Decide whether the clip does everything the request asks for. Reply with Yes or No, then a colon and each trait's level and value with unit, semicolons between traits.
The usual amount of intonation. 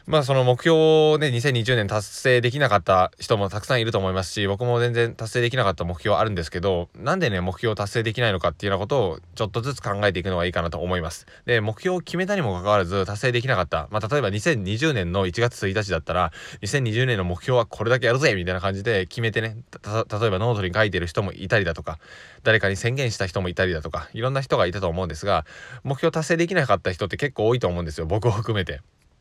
Yes: average, 4.7 semitones